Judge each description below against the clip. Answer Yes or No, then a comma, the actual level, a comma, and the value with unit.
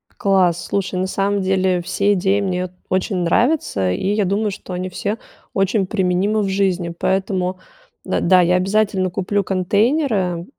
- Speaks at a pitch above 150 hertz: Yes, high, 190 Hz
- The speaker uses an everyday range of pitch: No, narrow, 1.8 semitones